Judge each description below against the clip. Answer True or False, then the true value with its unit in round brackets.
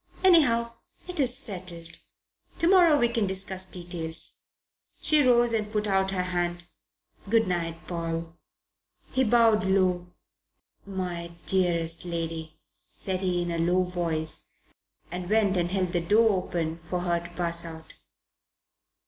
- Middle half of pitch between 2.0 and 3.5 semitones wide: False (3.9 semitones)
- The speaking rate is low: True (130 wpm)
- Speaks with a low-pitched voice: False (180 Hz)